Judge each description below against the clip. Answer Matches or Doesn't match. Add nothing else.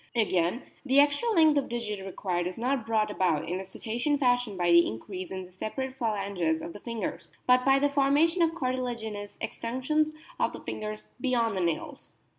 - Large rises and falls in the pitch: Matches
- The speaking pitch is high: Matches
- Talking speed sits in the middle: Matches